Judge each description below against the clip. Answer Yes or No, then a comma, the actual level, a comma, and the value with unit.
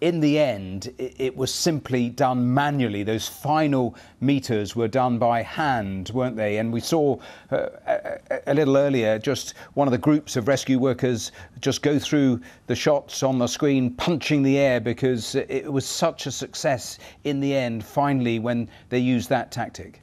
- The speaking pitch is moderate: No, low, 130 Hz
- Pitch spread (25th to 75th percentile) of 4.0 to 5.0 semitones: No, average, 3.2 semitones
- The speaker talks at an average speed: Yes, average, 175 wpm